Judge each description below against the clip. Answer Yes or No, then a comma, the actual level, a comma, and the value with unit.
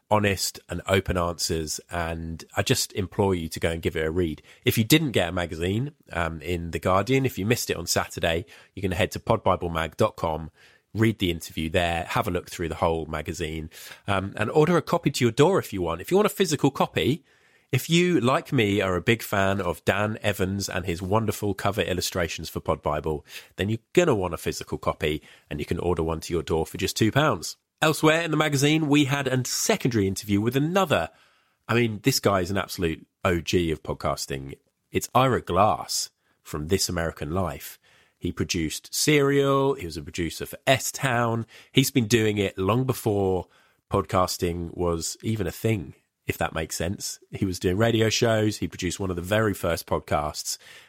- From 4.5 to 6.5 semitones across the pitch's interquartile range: Yes, wide, 5.6 semitones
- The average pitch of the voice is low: Yes, very low, 95 Hz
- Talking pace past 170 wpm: Yes, average, 200 wpm